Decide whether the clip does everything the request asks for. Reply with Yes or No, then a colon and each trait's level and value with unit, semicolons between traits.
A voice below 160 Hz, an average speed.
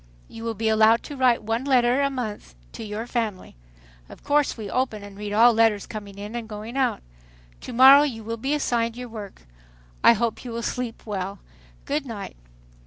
No: high, 230 Hz; average, 195 wpm